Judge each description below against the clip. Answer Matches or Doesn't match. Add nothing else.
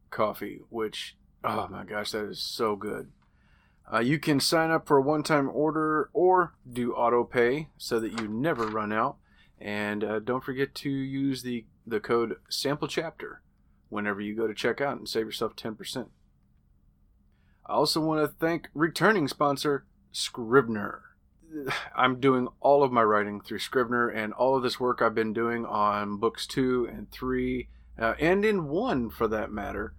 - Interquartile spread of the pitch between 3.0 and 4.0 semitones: Doesn't match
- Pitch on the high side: Doesn't match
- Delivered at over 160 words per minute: Matches